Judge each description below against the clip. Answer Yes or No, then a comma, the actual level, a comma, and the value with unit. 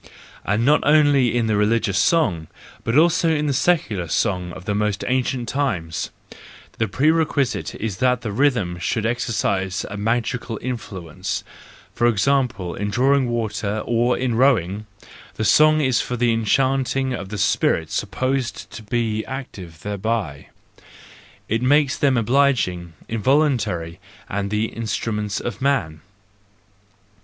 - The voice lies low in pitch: Yes, low, 115 Hz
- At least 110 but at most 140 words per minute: Yes, slow, 135 wpm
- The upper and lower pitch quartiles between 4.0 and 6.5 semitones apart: Yes, average, 4.5 semitones